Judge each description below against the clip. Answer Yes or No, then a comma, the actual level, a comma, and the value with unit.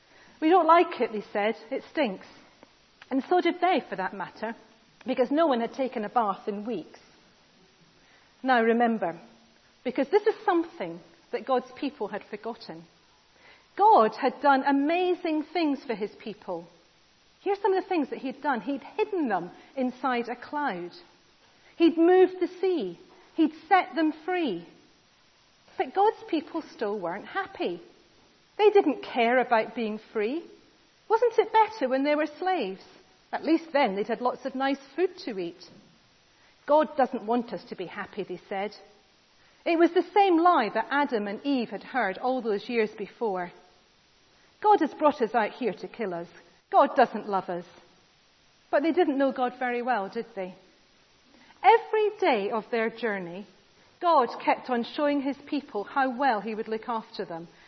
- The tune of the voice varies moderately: No, wide, 7.4 semitones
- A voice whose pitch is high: Yes, very high, 255 Hz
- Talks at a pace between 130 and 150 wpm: No, average, 165 wpm